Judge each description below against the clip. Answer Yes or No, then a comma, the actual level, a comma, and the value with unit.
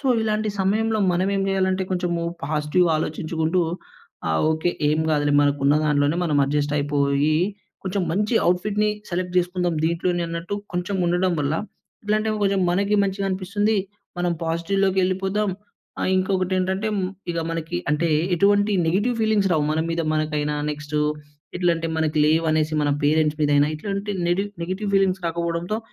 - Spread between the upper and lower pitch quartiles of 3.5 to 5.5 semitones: Yes, average, 3.9 semitones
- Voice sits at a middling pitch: Yes, medium, 175 Hz